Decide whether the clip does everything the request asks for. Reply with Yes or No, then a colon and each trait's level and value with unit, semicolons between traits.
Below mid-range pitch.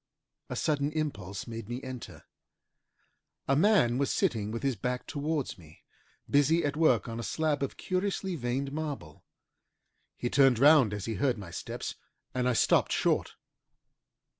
Yes: low, 130 Hz